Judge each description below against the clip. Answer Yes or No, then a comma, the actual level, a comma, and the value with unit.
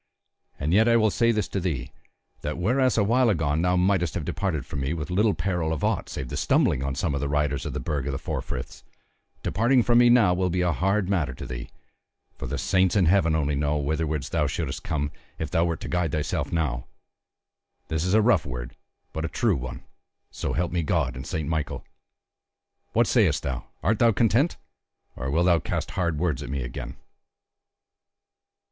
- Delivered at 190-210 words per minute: Yes, fast, 205 wpm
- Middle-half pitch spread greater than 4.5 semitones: Yes, average, 5.1 semitones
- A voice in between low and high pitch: No, very low, 80 Hz